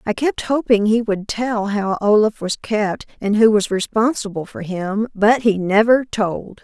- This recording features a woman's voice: Yes, female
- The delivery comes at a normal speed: Yes, average, 180 wpm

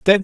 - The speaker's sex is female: No, male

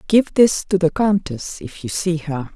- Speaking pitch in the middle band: Yes, medium, 175 Hz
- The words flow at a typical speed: No, fast, 210 wpm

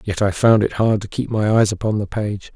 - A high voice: No, low, 105 Hz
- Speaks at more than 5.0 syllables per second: Yes, 5.3 syllables/s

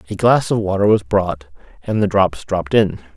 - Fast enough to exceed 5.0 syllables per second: Yes, 5.2 syllables/s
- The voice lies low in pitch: Yes, low, 105 Hz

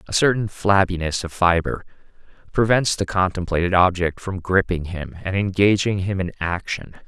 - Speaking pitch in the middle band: No, very low, 95 Hz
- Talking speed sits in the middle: Yes, average, 145 wpm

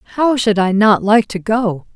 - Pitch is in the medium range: No, high, 215 Hz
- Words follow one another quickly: Yes, fast, 215 wpm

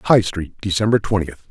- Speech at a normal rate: Yes, average, 160 wpm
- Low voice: Yes, low, 100 Hz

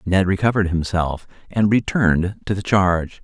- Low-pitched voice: Yes, very low, 95 Hz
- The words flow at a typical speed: Yes, average, 150 wpm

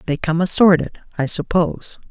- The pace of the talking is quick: No, average, 140 wpm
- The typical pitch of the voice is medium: Yes, medium, 165 Hz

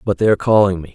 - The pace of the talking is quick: Yes, fast, 315 wpm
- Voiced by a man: Yes, male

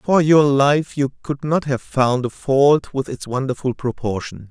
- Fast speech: No, average, 185 wpm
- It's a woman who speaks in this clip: No, male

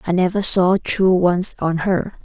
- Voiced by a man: No, female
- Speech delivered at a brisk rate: No, average, 190 wpm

